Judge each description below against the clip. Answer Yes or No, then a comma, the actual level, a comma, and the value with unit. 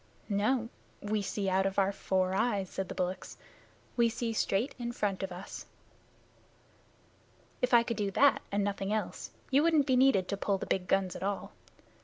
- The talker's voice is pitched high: Yes, high, 200 Hz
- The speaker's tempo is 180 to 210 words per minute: Yes, average, 185 wpm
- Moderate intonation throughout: Yes, average, 3.5 semitones